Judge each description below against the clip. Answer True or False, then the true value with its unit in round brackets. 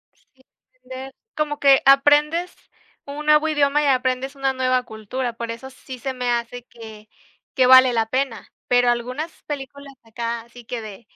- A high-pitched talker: True (255 Hz)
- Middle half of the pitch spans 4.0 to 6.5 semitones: False (2.7 semitones)